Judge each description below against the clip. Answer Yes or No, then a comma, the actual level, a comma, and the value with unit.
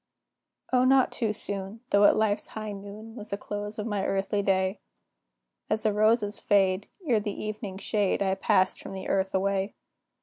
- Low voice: No, high, 205 Hz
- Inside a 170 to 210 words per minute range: Yes, average, 175 wpm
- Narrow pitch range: Yes, narrow, 1.8 semitones